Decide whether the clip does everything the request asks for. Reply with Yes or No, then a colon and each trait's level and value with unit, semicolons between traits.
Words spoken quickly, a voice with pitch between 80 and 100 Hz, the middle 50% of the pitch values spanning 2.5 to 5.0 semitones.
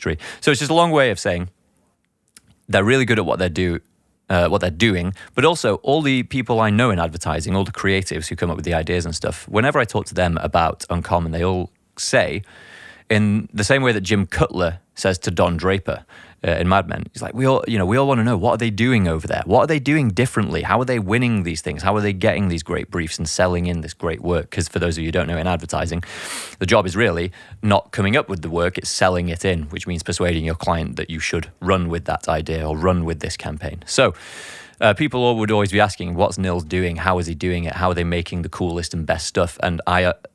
Yes: fast, 260 wpm; very low, 90 Hz; average, 3.6 semitones